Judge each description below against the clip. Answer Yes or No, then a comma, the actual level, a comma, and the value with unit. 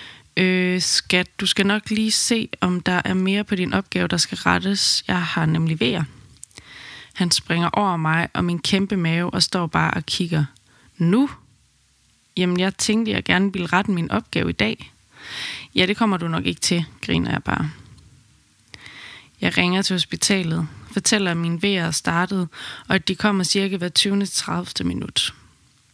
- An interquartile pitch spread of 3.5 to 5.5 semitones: No, average, 2.7 semitones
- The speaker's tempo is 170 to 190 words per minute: Yes, average, 175 wpm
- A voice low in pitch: No, medium, 180 Hz